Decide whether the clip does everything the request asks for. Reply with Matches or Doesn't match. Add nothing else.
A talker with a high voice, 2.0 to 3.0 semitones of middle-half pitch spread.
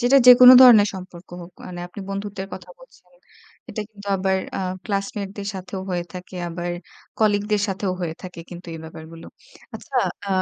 Matches